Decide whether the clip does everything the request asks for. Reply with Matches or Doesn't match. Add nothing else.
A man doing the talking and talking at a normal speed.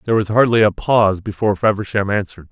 Matches